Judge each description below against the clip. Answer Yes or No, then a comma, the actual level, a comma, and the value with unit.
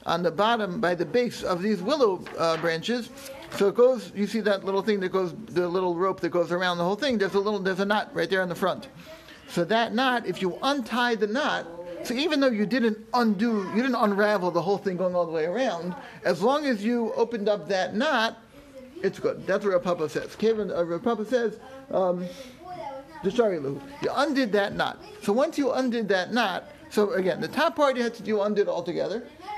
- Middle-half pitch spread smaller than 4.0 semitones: No, average, 5.0 semitones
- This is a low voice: No, high, 210 Hz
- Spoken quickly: Yes, fast, 215 wpm